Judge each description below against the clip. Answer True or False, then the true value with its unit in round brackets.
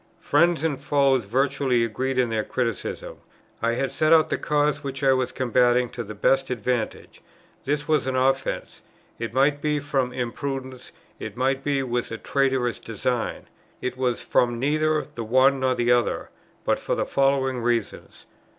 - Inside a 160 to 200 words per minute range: True (170 wpm)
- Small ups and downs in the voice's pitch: True (2.3 semitones)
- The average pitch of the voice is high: False (130 Hz)